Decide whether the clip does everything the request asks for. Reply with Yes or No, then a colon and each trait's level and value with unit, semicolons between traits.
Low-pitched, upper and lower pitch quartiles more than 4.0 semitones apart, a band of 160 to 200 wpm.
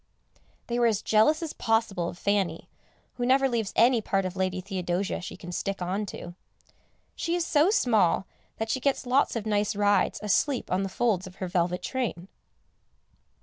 No: high, 205 Hz; average, 4.5 semitones; average, 180 wpm